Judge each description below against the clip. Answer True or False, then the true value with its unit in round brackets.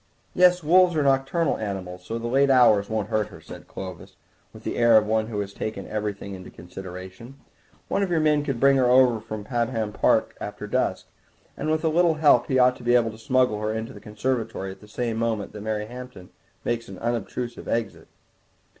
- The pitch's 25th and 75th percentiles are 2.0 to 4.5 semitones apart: True (3.9 semitones)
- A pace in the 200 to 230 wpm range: True (205 wpm)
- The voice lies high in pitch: False (115 Hz)